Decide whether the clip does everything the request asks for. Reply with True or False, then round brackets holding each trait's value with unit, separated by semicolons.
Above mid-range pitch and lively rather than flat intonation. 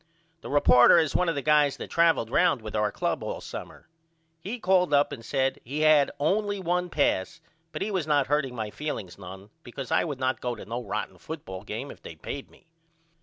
False (140 Hz; 6.2 semitones)